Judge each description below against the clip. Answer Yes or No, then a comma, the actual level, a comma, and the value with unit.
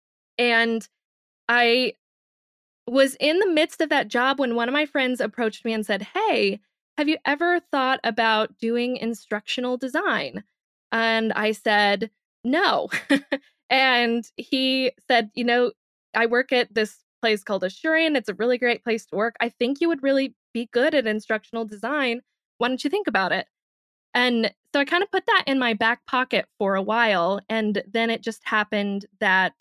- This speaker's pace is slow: No, average, 175 wpm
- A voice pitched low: No, high, 240 Hz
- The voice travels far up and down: No, average, 3.6 semitones